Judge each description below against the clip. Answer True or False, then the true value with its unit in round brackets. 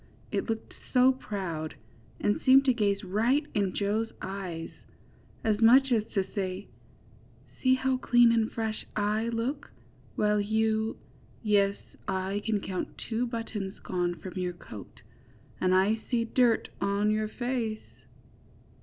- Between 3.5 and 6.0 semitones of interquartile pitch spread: False (2.8 semitones)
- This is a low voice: False (215 Hz)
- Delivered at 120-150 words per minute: True (135 wpm)